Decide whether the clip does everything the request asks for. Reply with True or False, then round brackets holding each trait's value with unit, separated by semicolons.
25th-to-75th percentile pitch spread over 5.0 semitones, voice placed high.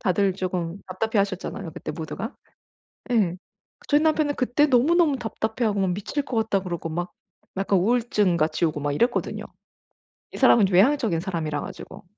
True (5.5 semitones; 195 Hz)